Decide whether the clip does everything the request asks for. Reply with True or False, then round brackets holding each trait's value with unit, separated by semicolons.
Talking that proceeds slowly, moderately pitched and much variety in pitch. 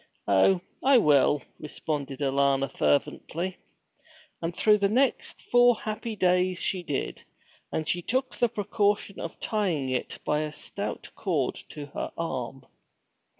True (130 wpm; 170 Hz; 6.8 semitones)